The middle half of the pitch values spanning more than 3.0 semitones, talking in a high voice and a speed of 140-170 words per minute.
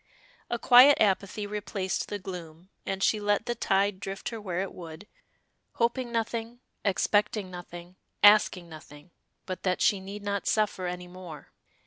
No: average, 2.7 semitones; high, 195 Hz; average, 150 wpm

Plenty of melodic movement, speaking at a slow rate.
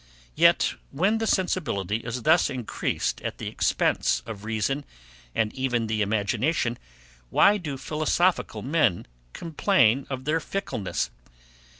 Yes: wide, 6.7 semitones; slow, 120 wpm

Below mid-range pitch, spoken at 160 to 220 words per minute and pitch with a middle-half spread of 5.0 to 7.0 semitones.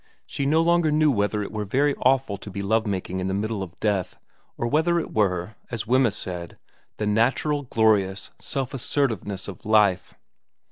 Yes: low, 110 Hz; average, 180 wpm; average, 5.3 semitones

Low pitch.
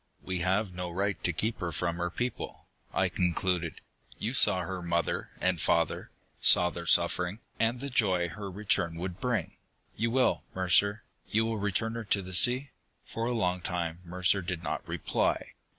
Yes: very low, 95 Hz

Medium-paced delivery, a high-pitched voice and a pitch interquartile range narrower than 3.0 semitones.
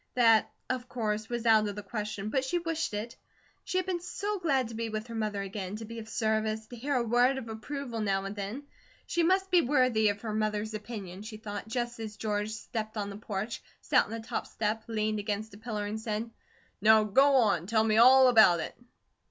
No: fast, 225 wpm; high, 220 Hz; narrow, 2.5 semitones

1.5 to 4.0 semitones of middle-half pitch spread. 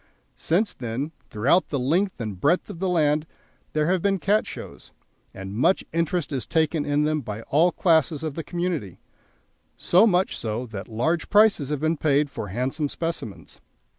No: average, 5.2 semitones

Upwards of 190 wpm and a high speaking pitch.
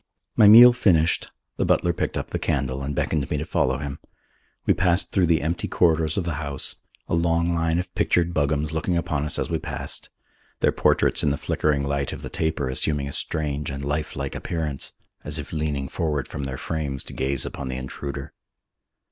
No: average, 200 wpm; very low, 75 Hz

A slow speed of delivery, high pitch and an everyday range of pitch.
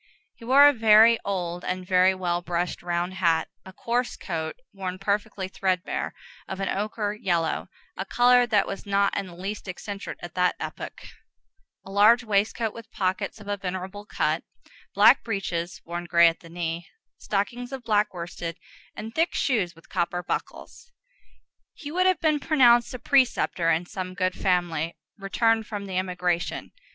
No: average, 165 wpm; high, 195 Hz; average, 4.0 semitones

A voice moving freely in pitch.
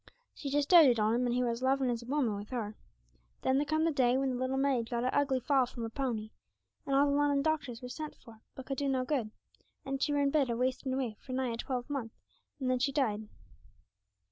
No: narrow, 2.6 semitones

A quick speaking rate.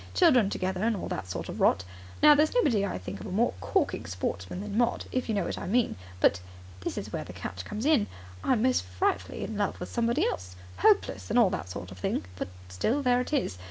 Yes: fast, 230 wpm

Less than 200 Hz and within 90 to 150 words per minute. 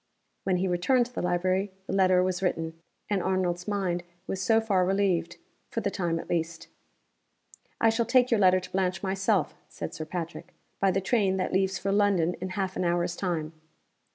No: medium, 185 Hz; average, 190 wpm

